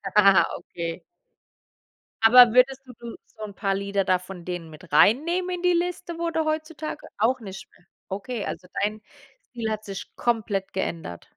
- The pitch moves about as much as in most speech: No, wide, 5.9 semitones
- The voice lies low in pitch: No, high, 215 Hz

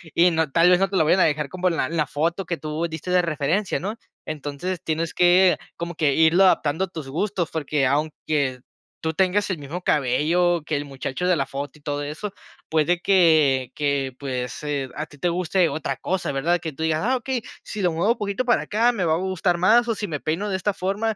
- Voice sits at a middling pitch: Yes, medium, 165 Hz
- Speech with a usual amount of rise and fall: Yes, average, 3.9 semitones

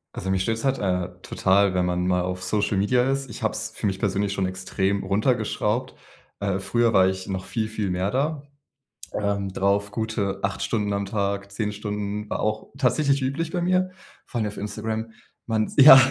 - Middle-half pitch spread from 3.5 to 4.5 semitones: No, average, 2.7 semitones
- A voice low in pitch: Yes, low, 105 Hz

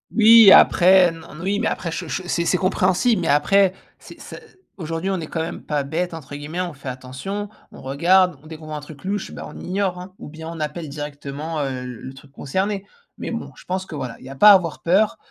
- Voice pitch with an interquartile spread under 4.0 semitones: No, average, 4.4 semitones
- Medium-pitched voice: Yes, medium, 165 Hz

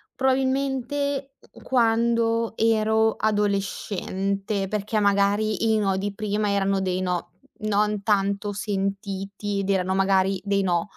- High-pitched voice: Yes, high, 205 Hz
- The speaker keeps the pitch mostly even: Yes, narrow, 2.1 semitones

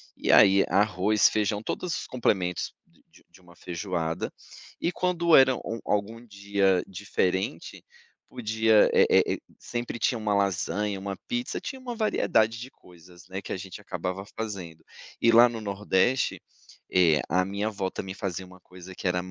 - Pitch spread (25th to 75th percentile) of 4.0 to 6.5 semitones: No, average, 3.3 semitones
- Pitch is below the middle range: Yes, low, 100 Hz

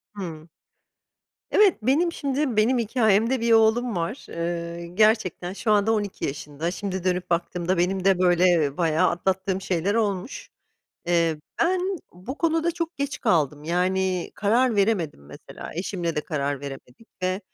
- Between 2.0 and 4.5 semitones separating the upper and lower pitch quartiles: No, average, 4.9 semitones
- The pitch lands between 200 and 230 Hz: No, high, 190 Hz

